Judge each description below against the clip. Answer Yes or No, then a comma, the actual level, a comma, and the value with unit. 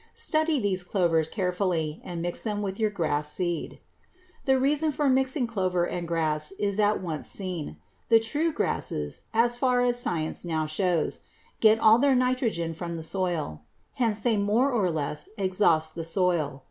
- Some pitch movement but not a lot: No, wide, 6.1 semitones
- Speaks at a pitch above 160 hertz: Yes, high, 190 Hz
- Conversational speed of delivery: Yes, average, 165 wpm